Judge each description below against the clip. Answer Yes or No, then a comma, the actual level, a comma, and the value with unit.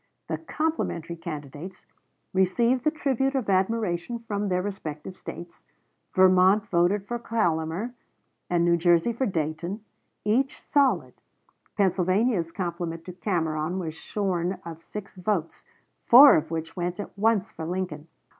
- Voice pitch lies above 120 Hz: Yes, medium, 185 Hz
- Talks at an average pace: No, slow, 130 wpm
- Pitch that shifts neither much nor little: Yes, average, 4.2 semitones